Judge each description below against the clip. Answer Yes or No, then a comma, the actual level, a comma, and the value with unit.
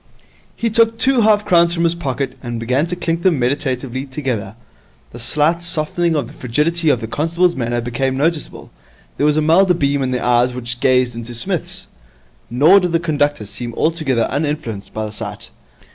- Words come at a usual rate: Yes, average, 185 wpm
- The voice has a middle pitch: Yes, medium, 145 Hz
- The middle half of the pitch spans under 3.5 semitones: No, wide, 5.6 semitones